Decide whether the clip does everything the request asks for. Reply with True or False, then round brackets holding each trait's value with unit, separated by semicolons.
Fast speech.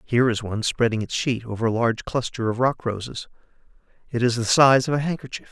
True (220 wpm)